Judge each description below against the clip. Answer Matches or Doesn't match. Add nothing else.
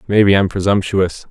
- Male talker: Matches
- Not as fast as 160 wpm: Matches